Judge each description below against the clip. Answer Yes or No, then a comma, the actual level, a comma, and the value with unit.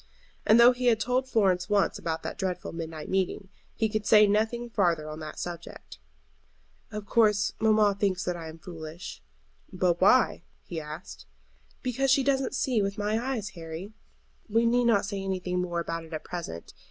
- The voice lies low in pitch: No, high, 195 Hz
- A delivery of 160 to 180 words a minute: Yes, average, 175 wpm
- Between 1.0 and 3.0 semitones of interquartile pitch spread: No, average, 4.7 semitones